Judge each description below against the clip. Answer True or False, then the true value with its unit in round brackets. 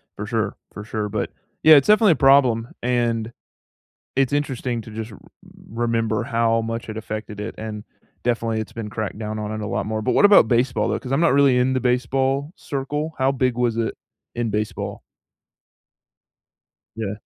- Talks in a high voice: False (115 Hz)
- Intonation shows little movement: False (3.2 semitones)